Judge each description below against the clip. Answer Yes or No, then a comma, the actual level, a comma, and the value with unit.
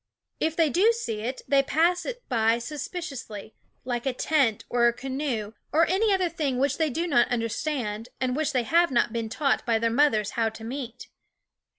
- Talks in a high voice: Yes, very high, 260 Hz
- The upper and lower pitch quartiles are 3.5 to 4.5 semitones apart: No, average, 5.3 semitones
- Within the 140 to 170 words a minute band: No, average, 195 wpm